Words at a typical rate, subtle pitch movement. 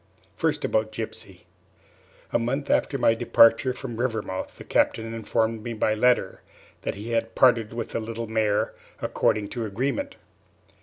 Yes: average, 150 wpm; narrow, 1.7 semitones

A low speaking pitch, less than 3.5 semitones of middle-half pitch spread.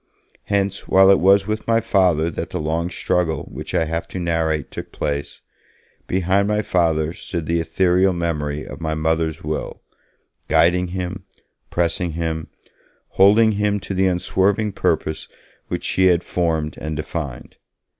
Yes: very low, 85 Hz; average, 3.1 semitones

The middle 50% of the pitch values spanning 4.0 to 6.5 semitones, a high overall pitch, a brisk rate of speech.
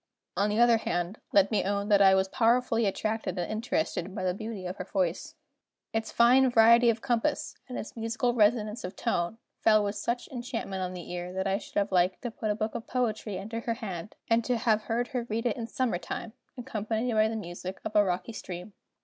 No: average, 3.3 semitones; high, 215 Hz; fast, 220 wpm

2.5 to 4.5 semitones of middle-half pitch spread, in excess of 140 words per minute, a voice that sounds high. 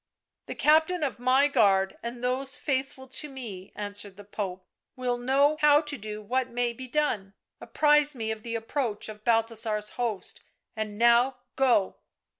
Yes: average, 4.1 semitones; average, 175 wpm; high, 240 Hz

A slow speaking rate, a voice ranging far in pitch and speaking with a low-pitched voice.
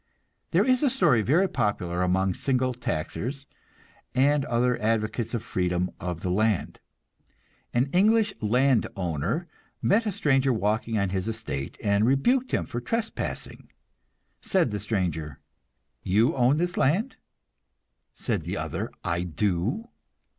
Yes: slow, 130 wpm; wide, 7.4 semitones; low, 115 Hz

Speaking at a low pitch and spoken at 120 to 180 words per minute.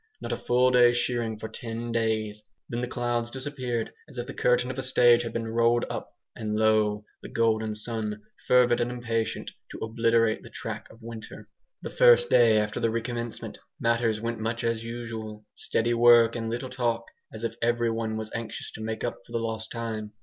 No: low, 115 Hz; average, 195 wpm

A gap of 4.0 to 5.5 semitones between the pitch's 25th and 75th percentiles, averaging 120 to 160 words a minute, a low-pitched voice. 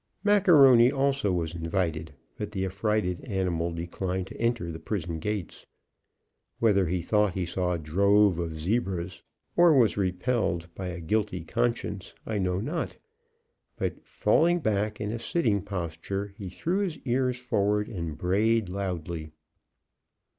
Yes: average, 4.6 semitones; average, 140 wpm; low, 100 Hz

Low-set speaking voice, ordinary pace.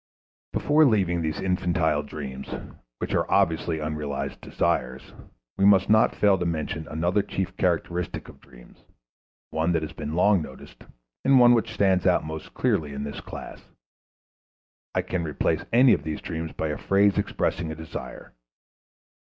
Yes: very low, 80 Hz; average, 155 wpm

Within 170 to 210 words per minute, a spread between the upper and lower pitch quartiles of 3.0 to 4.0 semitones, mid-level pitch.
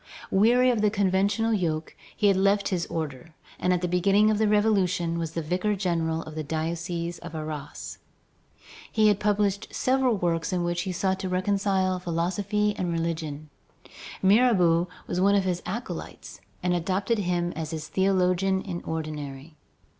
No: average, 160 wpm; average, 3.3 semitones; medium, 180 Hz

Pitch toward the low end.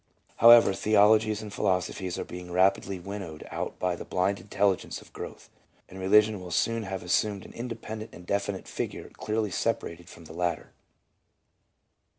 Yes: low, 100 Hz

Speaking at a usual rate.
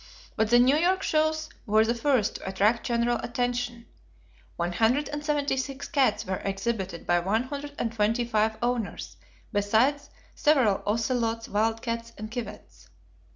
Yes: average, 155 wpm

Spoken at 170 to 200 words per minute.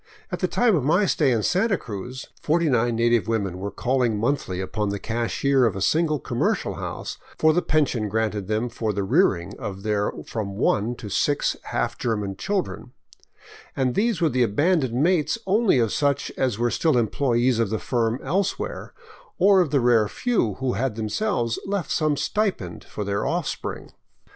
Yes: average, 175 wpm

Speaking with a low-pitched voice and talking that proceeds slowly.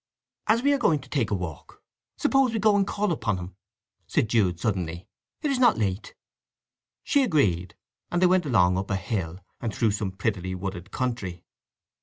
No: low, 110 Hz; average, 185 wpm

